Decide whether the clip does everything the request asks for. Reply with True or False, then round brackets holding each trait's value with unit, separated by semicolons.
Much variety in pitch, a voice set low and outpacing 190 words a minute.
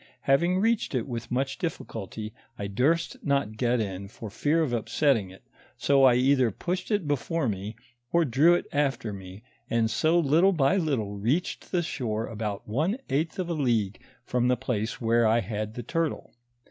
False (6.3 semitones; 125 Hz; 180 wpm)